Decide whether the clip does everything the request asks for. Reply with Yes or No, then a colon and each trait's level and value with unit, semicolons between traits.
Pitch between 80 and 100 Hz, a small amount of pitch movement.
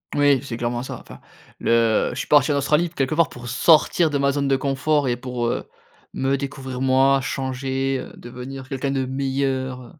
No: low, 135 Hz; narrow, 1.5 semitones